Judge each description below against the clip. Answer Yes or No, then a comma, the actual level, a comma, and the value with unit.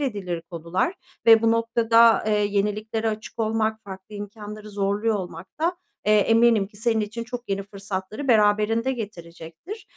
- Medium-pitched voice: No, high, 215 Hz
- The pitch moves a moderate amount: No, narrow, 2.3 semitones